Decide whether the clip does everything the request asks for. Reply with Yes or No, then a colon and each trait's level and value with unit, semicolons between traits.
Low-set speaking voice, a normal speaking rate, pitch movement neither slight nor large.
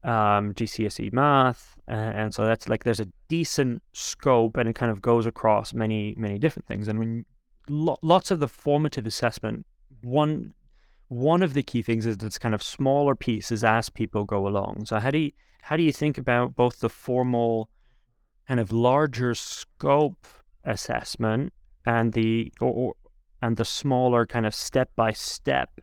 Yes: low, 115 Hz; average, 175 wpm; average, 3.4 semitones